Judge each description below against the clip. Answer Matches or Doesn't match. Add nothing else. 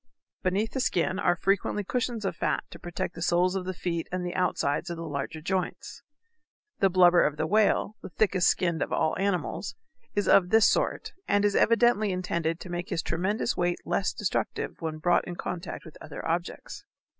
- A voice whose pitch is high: Doesn't match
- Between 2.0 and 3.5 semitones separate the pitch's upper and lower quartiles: Matches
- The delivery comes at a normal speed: Matches